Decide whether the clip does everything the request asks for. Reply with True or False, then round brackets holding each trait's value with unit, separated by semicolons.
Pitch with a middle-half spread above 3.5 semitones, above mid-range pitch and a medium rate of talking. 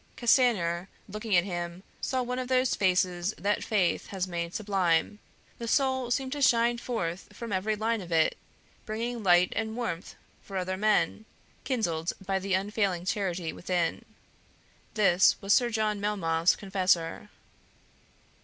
True (4.3 semitones; 200 Hz; 145 wpm)